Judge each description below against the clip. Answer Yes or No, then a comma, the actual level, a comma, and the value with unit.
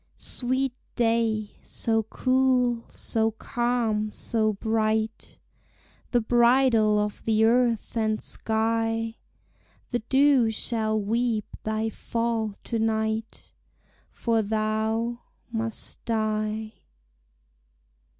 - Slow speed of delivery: Yes, slow, 90 wpm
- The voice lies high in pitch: Yes, high, 225 Hz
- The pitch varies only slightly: Yes, narrow, 1.5 semitones